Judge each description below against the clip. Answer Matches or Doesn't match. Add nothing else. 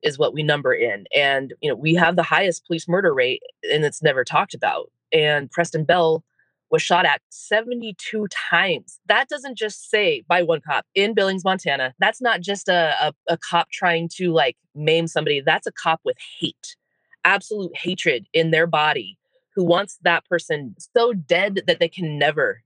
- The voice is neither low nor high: Matches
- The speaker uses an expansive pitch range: Doesn't match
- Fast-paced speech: Doesn't match